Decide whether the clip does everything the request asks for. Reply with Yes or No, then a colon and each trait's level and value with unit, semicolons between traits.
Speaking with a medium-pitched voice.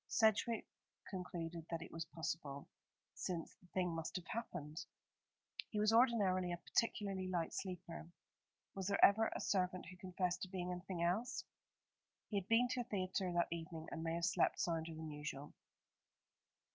Yes: medium, 180 Hz